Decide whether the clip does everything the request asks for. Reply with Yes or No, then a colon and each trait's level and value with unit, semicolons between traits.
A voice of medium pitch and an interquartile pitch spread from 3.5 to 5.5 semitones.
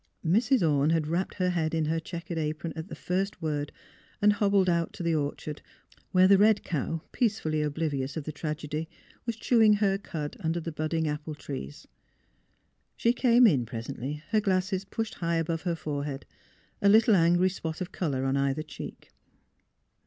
Yes: medium, 165 Hz; average, 4.2 semitones